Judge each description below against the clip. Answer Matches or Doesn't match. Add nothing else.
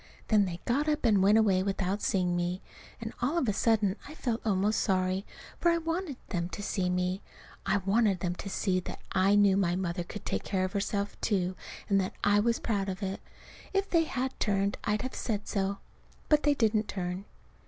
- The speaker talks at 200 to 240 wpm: Matches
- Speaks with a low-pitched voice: Doesn't match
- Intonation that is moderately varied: Matches